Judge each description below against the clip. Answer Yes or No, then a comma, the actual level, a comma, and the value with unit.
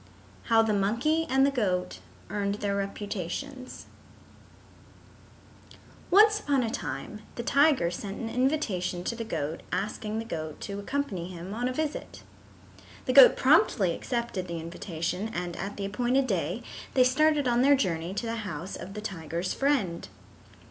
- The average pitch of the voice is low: No, high, 210 Hz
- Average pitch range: No, wide, 6.1 semitones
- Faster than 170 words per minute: No, average, 155 wpm